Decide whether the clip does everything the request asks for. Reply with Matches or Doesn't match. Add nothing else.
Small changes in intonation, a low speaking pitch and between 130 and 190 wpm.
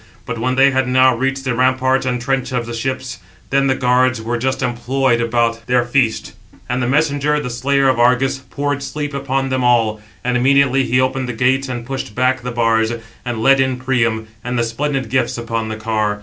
Doesn't match